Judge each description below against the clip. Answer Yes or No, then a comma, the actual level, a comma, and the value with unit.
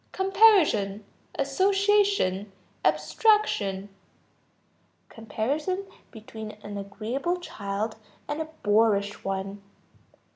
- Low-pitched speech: No, high, 220 Hz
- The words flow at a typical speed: No, slow, 70 wpm